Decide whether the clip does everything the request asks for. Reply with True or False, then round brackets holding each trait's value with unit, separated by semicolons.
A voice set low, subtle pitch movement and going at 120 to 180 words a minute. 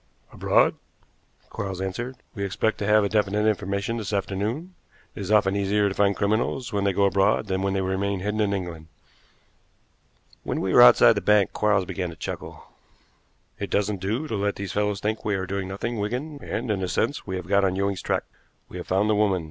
False (100 Hz; 1.7 semitones; 205 wpm)